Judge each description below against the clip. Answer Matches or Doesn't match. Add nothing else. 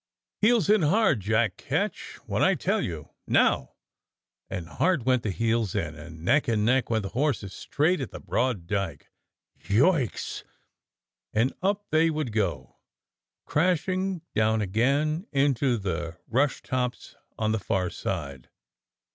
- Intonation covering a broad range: Matches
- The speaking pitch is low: Matches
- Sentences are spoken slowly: Doesn't match